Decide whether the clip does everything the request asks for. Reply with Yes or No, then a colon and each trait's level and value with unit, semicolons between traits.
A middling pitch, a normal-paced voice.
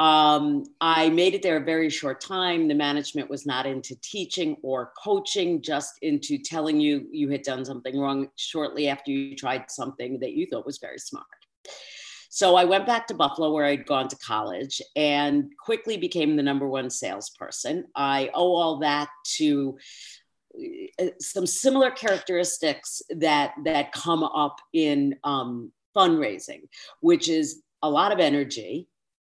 Yes: medium, 155 Hz; average, 155 wpm